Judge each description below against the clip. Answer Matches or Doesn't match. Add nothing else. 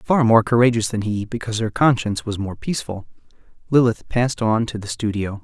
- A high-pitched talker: Doesn't match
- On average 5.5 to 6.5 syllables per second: Matches